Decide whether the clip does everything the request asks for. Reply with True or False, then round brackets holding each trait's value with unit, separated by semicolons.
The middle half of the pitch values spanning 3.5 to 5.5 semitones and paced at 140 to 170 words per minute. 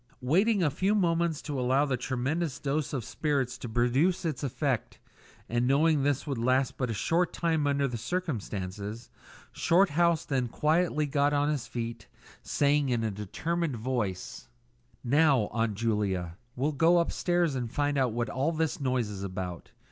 True (4.9 semitones; 165 wpm)